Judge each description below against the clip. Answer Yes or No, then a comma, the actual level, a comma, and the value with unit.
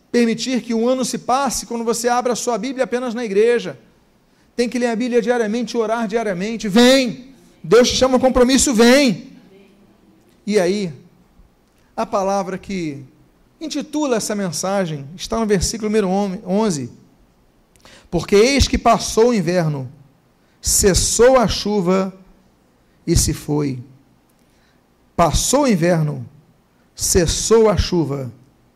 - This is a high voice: Yes, high, 215 Hz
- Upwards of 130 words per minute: No, average, 125 wpm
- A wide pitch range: Yes, wide, 6.0 semitones